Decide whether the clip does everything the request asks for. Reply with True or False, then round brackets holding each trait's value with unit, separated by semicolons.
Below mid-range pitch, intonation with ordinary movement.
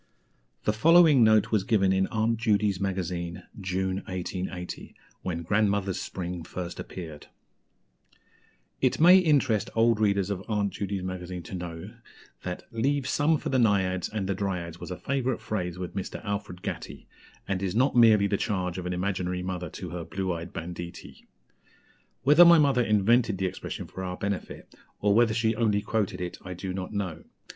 True (95 Hz; 3.5 semitones)